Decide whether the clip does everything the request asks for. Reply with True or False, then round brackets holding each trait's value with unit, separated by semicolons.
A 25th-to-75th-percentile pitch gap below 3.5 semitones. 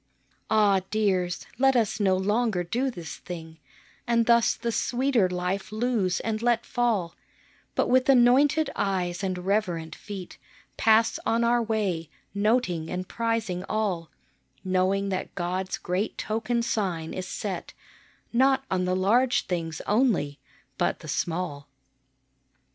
False (4.4 semitones)